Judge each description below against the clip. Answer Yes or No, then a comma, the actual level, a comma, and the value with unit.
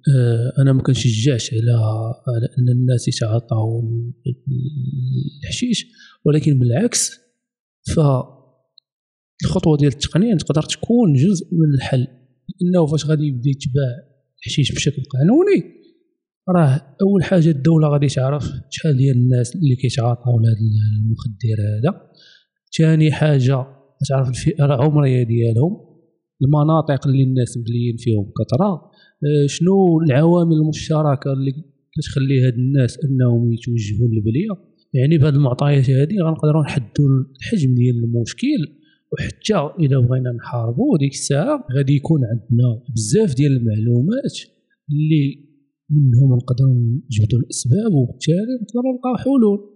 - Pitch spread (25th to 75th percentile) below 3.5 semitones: No, average, 4.2 semitones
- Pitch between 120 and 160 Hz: Yes, medium, 140 Hz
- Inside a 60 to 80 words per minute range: No, average, 110 wpm